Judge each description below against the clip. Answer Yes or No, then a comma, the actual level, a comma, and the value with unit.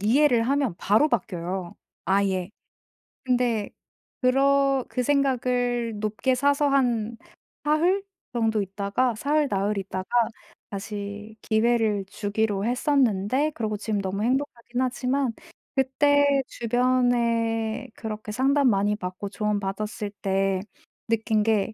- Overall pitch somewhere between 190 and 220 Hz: No, high, 230 Hz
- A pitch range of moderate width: Yes, average, 4.1 semitones